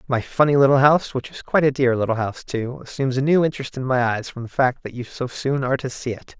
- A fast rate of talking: Yes, fast, 280 wpm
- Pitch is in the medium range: No, low, 130 Hz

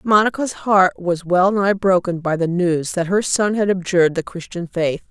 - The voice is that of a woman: Yes, female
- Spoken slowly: No, average, 200 wpm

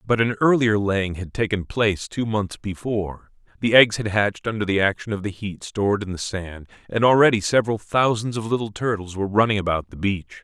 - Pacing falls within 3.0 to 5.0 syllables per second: No, 5.6 syllables/s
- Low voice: Yes, low, 105 Hz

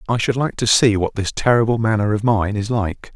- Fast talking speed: Yes, fast, 245 wpm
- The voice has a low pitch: Yes, low, 110 Hz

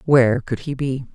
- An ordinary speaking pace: No, fast, 210 wpm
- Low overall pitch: Yes, low, 130 Hz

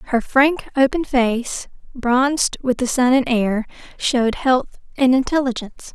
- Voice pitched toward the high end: Yes, very high, 255 Hz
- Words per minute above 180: No, average, 140 wpm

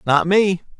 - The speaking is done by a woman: No, male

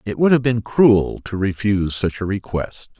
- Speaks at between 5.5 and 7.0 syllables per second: No, 4.7 syllables/s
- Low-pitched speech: Yes, low, 105 Hz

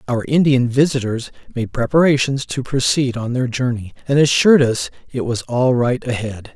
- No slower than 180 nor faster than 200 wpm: No, average, 165 wpm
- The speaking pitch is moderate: No, low, 125 Hz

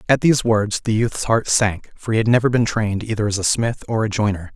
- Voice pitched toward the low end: Yes, low, 110 Hz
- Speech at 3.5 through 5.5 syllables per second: No, 5.8 syllables/s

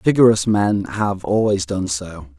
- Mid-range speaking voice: No, very low, 95 Hz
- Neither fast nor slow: Yes, average, 150 wpm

